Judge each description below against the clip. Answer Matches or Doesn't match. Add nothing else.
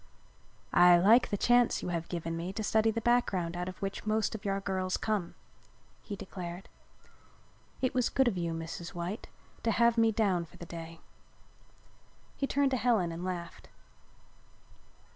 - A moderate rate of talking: Matches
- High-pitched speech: Matches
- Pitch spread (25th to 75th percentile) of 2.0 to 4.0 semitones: Doesn't match